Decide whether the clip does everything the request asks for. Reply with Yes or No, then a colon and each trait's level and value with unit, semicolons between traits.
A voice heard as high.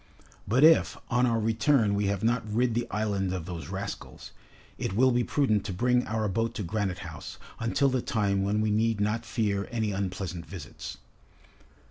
No: low, 110 Hz